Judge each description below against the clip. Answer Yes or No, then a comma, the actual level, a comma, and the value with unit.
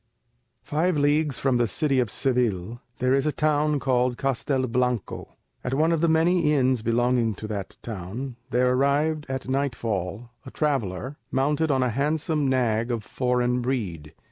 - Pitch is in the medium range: No, low, 130 Hz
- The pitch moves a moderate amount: Yes, average, 3.5 semitones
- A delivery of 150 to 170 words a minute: Yes, average, 155 wpm